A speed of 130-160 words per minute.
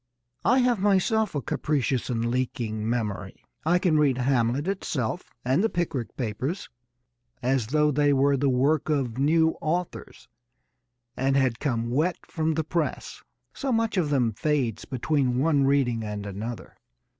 Yes: average, 150 wpm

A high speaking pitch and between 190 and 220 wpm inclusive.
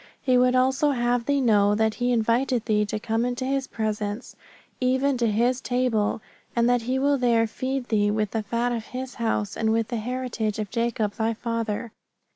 Yes: high, 235 Hz; average, 195 wpm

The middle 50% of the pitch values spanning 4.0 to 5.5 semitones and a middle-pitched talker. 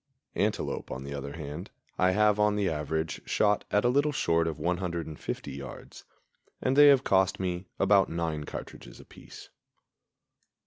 No: average, 4.7 semitones; very low, 90 Hz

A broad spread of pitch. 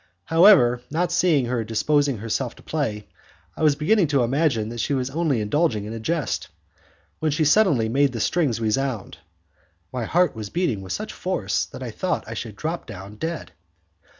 Yes: wide, 5.9 semitones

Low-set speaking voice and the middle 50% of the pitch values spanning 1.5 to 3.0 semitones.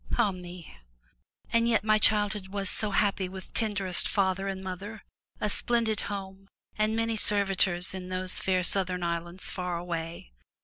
No: high, 190 Hz; narrow, 2.4 semitones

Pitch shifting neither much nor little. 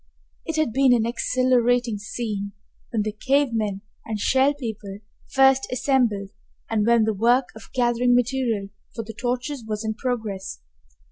Yes: average, 3.0 semitones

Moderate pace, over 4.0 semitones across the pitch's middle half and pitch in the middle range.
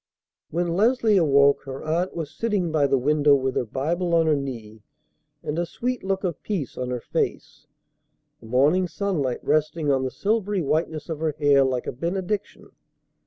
Yes: average, 175 wpm; average, 4.8 semitones; medium, 155 Hz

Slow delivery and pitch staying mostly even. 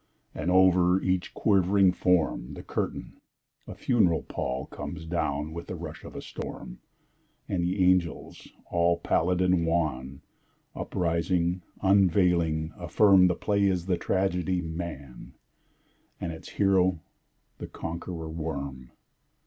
Yes: slow, 125 wpm; narrow, 2.3 semitones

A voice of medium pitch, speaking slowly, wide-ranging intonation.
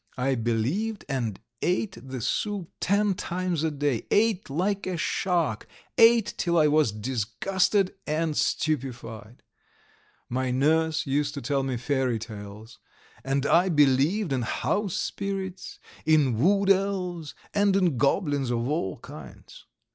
Yes: medium, 150 Hz; slow, 130 wpm; wide, 6.6 semitones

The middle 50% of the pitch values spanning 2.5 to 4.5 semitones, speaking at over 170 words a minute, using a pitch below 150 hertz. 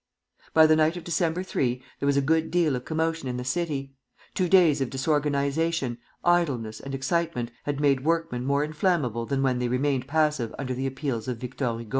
Yes: average, 4.0 semitones; average, 195 wpm; medium, 140 Hz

